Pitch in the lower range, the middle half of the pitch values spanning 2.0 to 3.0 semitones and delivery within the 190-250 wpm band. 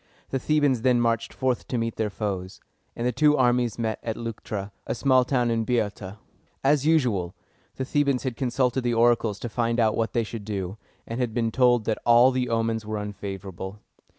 Yes: low, 115 Hz; narrow, 2.6 semitones; average, 195 wpm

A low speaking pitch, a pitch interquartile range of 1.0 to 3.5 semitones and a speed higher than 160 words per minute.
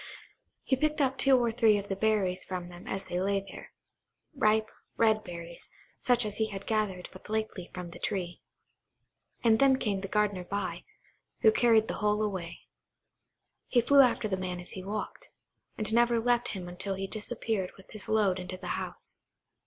No: high, 210 Hz; average, 3.0 semitones; average, 175 wpm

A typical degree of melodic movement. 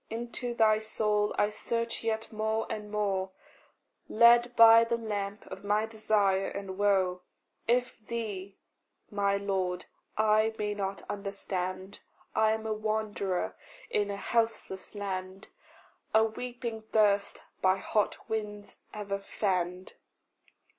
No: narrow, 2.0 semitones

